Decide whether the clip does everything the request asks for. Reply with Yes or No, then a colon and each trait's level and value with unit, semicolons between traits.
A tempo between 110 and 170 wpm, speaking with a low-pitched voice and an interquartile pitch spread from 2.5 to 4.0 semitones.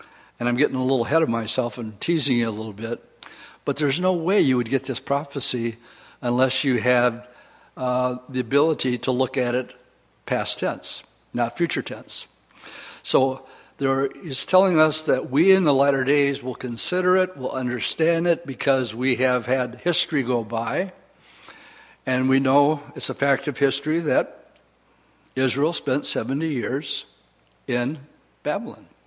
Yes: average, 160 wpm; low, 130 Hz; average, 2.8 semitones